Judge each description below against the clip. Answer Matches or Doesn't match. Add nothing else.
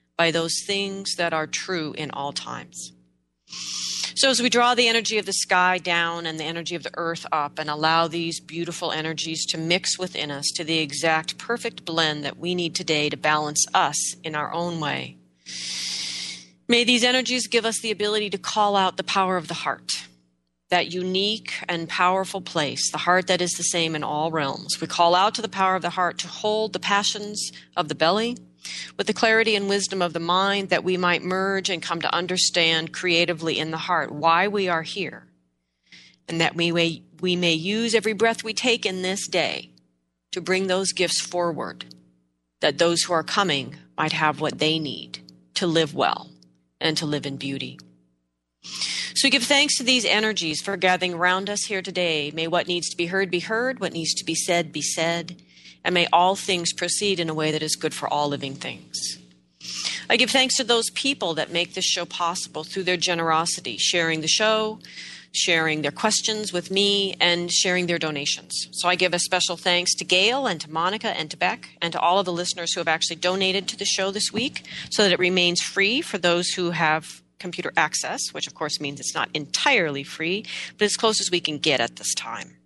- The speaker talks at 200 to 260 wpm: Matches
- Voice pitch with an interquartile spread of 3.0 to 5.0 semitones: Matches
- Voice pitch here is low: Doesn't match